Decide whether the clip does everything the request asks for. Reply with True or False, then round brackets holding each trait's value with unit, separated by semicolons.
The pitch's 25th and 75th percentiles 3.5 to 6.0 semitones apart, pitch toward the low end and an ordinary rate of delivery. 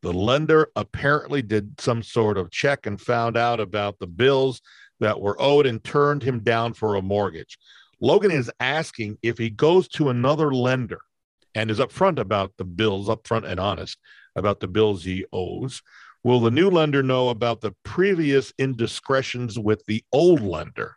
True (4.3 semitones; 115 Hz; 170 wpm)